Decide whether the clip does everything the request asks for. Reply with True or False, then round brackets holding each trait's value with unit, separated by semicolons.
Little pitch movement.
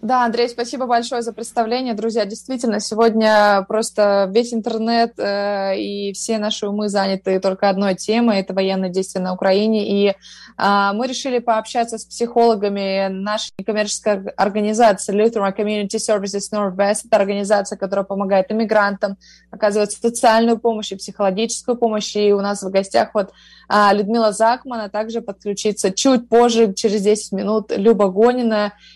True (2.3 semitones)